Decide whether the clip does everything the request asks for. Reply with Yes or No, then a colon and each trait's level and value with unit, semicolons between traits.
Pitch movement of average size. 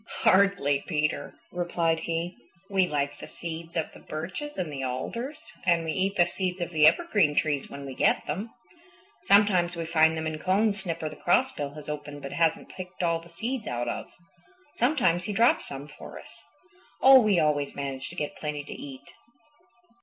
Yes: average, 4.2 semitones